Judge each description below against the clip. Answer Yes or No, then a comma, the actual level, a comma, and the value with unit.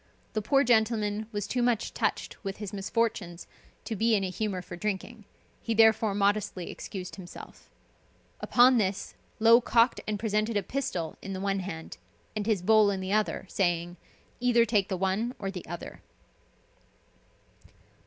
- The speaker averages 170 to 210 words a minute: No, average, 160 wpm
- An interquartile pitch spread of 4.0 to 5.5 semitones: No, average, 2.9 semitones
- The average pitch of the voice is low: No, high, 210 Hz